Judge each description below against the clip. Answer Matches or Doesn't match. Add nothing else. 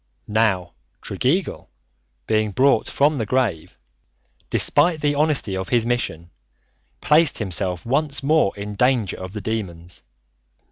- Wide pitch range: Matches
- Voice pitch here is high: Doesn't match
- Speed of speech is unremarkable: Doesn't match